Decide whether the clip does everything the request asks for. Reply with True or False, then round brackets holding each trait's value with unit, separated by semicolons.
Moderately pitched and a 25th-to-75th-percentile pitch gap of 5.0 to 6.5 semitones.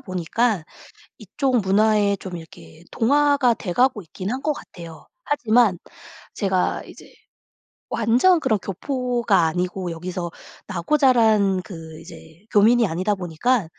False (200 Hz; 5.4 semitones)